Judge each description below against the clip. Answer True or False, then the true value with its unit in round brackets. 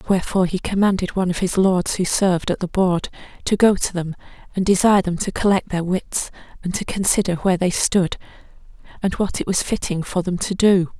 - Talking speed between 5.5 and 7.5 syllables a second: True (5.8 syllables/s)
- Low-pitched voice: False (185 Hz)